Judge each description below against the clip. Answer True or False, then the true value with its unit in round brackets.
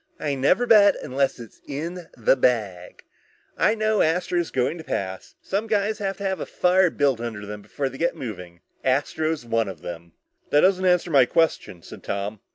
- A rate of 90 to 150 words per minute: False (185 wpm)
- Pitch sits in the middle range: True (145 Hz)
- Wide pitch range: True (8.2 semitones)